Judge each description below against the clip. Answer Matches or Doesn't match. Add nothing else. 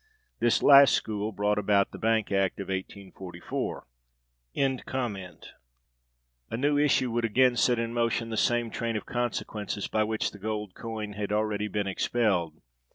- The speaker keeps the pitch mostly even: Doesn't match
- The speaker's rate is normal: Matches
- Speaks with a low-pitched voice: Matches